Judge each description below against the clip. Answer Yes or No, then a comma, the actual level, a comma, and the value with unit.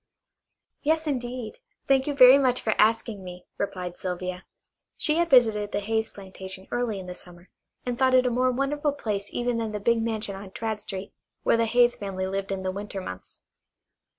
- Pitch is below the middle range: No, high, 220 Hz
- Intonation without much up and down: No, average, 4.5 semitones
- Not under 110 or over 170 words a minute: No, average, 190 wpm